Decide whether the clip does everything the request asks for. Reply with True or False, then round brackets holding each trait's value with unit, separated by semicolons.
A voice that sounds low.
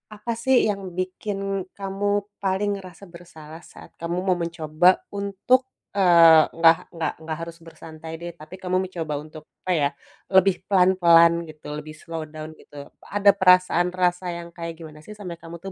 False (175 Hz)